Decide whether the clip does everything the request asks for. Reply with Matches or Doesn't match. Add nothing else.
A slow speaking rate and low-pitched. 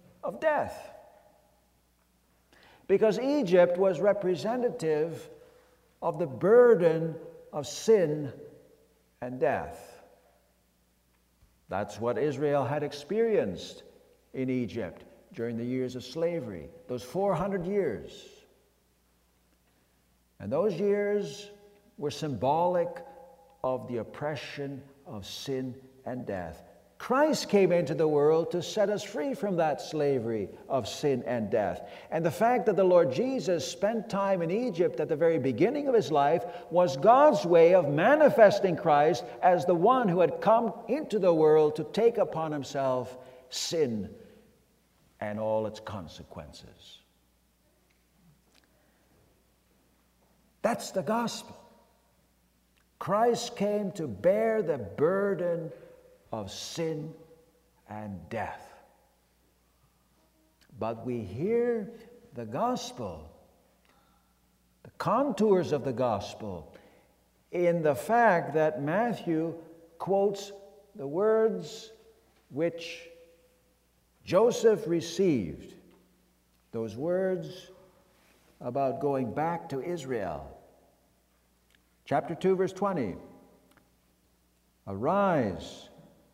Doesn't match